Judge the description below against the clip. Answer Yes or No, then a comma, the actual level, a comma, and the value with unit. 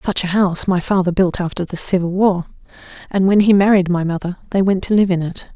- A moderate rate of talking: No, fast, 240 wpm